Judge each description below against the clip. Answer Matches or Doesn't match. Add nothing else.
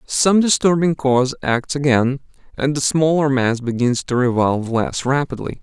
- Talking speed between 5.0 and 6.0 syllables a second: Doesn't match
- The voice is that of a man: Matches